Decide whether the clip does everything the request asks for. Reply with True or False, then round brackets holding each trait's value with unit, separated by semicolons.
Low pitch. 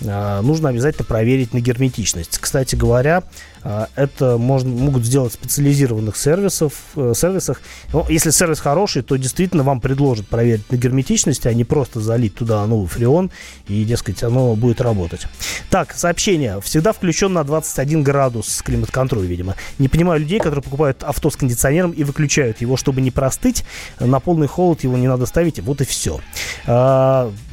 True (130 Hz)